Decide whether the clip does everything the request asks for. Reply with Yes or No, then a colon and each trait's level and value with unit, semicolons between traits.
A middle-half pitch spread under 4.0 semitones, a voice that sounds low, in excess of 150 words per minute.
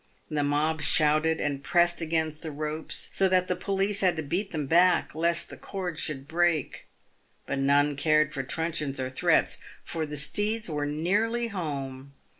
No: average, 3.1 semitones; medium, 155 Hz; average, 170 wpm